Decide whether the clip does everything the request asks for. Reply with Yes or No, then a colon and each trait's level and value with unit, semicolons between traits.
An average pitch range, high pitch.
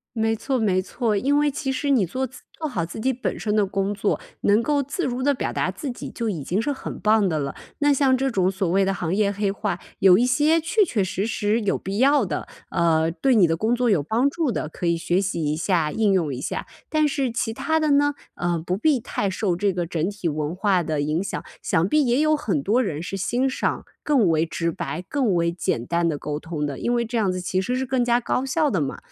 No: wide, 6.7 semitones; high, 205 Hz